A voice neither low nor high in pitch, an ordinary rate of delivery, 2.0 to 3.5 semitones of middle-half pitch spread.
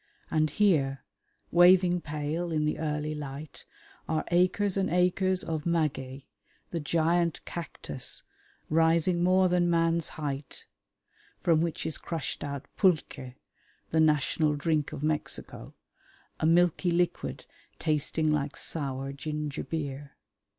No: medium, 160 Hz; slow, 120 wpm; average, 2.7 semitones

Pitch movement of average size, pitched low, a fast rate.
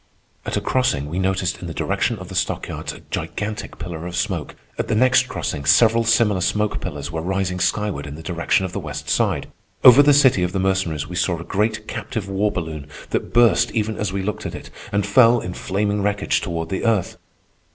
Yes: average, 3.9 semitones; very low, 95 Hz; fast, 215 wpm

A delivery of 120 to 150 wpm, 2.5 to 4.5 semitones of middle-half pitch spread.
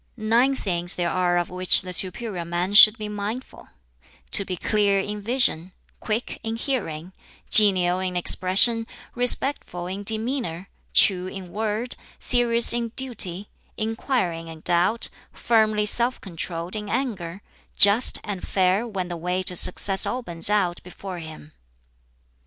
Yes: average, 140 wpm; average, 4.0 semitones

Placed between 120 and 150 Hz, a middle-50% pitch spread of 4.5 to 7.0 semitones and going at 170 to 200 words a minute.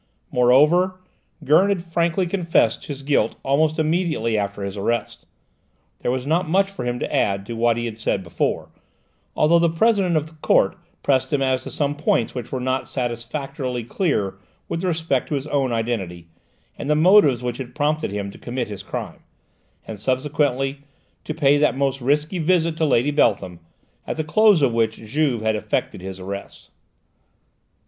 Yes: low, 135 Hz; average, 5.2 semitones; average, 175 wpm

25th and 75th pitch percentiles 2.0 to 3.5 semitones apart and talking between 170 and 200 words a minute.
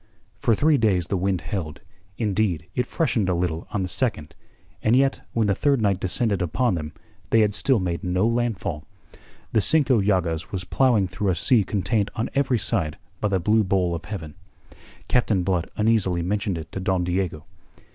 No: average, 4.0 semitones; average, 185 wpm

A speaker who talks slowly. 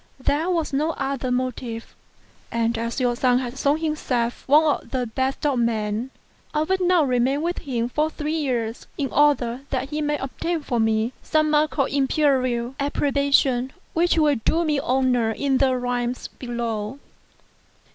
No: average, 170 wpm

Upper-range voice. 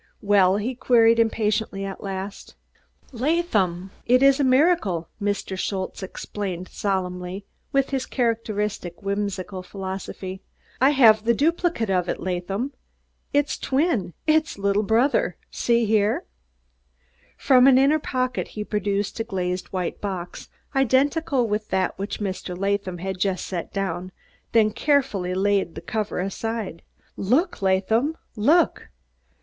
Yes: high, 205 Hz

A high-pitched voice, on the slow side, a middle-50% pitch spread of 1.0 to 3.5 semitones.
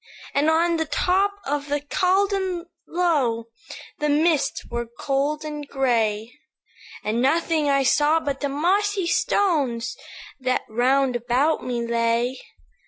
No: very high, 290 Hz; slow, 125 wpm; average, 5.2 semitones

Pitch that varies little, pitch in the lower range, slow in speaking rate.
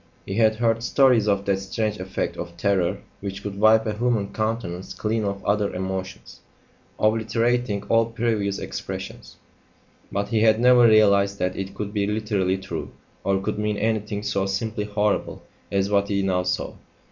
No: narrow, 2.1 semitones; low, 105 Hz; average, 165 wpm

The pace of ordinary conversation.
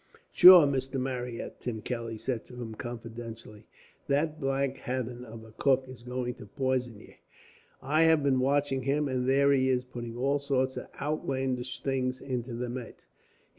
Yes: average, 170 wpm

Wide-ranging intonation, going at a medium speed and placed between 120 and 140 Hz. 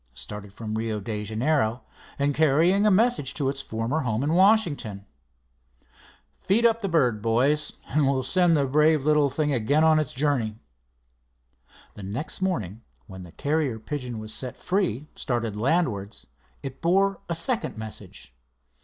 Yes: wide, 6.4 semitones; average, 155 wpm; low, 135 Hz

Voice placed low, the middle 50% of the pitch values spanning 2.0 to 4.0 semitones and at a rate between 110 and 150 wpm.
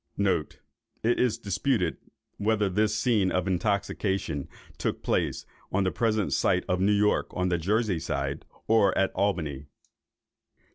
Yes: low, 100 Hz; average, 2.8 semitones; slow, 135 wpm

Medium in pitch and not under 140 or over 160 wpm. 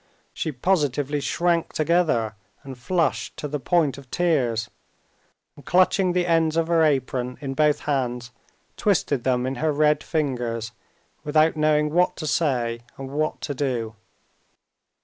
Yes: medium, 145 Hz; average, 145 wpm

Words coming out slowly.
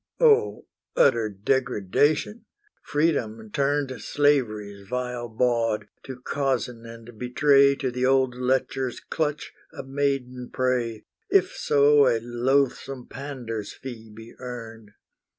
Yes: slow, 110 wpm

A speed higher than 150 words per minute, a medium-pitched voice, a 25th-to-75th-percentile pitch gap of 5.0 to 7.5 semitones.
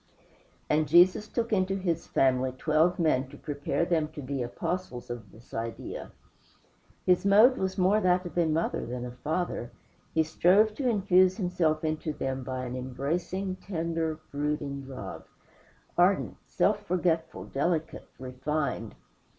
No: average, 145 wpm; medium, 160 Hz; wide, 5.4 semitones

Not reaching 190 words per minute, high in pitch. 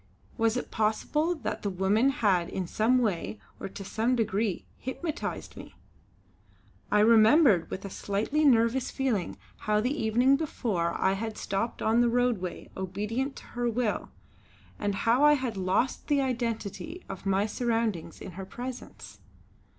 Yes: average, 150 wpm; high, 225 Hz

